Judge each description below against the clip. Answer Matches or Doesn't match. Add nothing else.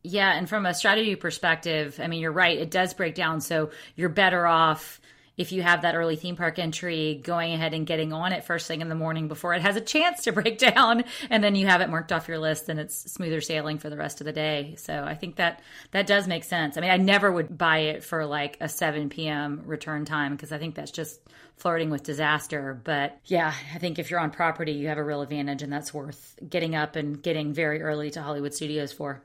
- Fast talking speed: Matches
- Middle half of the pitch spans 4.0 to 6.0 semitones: Doesn't match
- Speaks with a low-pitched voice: Doesn't match